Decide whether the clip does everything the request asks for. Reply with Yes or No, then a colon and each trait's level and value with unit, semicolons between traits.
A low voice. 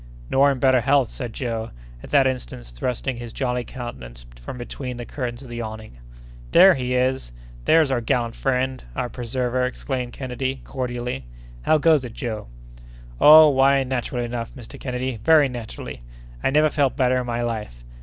Yes: low, 125 Hz